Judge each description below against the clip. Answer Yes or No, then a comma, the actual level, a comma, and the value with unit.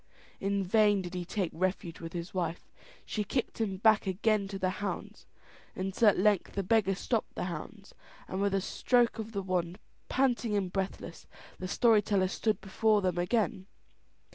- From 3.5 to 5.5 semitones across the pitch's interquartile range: No, average, 2.7 semitones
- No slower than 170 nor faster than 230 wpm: Yes, average, 175 wpm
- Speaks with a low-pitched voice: No, high, 195 Hz